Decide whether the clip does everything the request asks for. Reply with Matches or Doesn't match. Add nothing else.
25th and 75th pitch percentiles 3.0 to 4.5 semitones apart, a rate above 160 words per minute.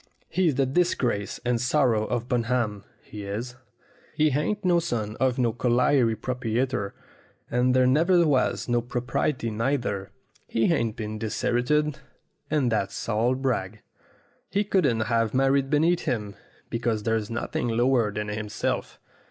Doesn't match